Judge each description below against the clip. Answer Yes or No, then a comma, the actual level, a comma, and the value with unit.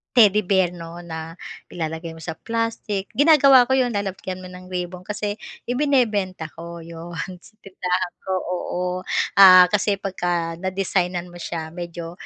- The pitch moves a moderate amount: Yes, average, 3.1 semitones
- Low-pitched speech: No, medium, 185 Hz